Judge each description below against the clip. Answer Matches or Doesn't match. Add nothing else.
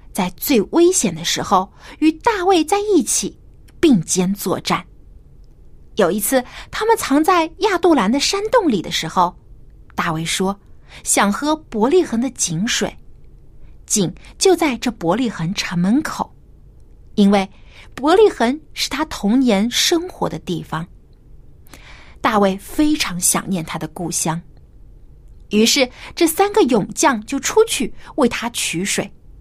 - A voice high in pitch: Matches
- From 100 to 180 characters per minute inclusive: Doesn't match